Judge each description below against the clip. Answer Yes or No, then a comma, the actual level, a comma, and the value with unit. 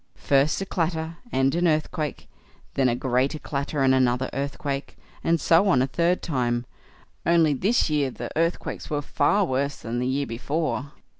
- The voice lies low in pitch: No, medium, 145 Hz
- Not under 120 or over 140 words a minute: No, average, 165 wpm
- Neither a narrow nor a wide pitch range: Yes, average, 3.8 semitones